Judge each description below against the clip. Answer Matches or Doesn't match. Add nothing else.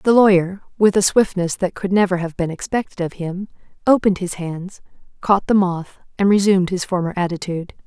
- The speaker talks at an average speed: Matches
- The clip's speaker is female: Matches